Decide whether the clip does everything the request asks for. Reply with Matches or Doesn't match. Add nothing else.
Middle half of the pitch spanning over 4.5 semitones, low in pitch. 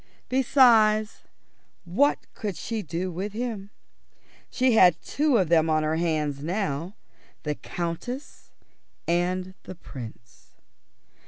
Doesn't match